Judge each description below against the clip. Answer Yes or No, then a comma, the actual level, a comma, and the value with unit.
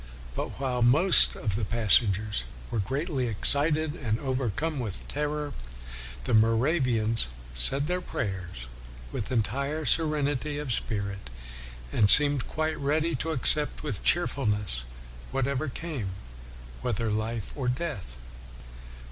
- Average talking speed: No, slow, 120 wpm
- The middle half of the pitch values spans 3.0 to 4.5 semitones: No, wide, 5.6 semitones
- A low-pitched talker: Yes, low, 130 Hz